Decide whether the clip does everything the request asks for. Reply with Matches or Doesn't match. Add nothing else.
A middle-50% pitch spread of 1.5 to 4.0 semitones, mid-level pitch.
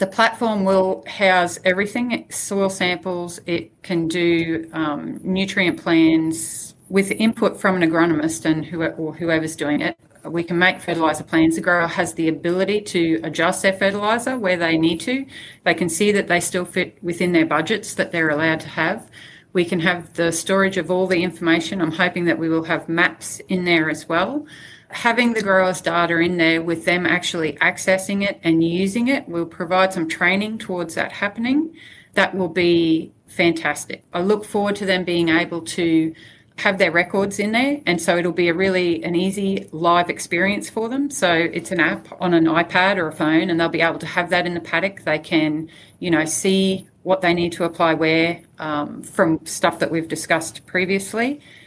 Matches